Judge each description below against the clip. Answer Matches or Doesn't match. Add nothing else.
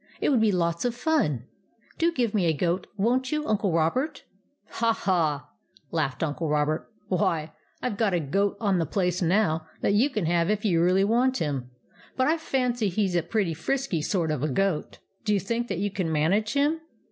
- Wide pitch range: Matches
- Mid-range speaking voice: Doesn't match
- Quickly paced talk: Matches